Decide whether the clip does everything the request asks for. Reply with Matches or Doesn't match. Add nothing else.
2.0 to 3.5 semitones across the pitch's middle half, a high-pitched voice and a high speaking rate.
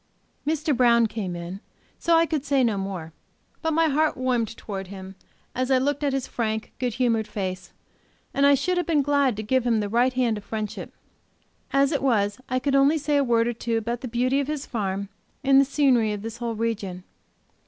Doesn't match